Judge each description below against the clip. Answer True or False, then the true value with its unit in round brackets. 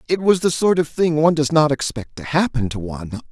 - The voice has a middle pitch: True (145 Hz)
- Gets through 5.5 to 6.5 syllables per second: True (5.9 syllables/s)